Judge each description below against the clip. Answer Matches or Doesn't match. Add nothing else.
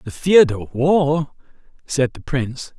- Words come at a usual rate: Matches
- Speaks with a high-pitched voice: Doesn't match